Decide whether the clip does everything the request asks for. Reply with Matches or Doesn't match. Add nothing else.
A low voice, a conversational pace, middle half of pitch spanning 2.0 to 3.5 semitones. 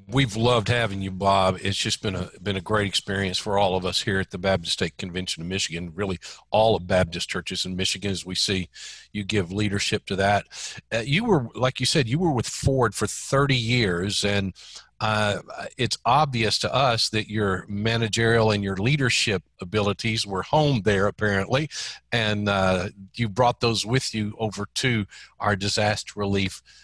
Matches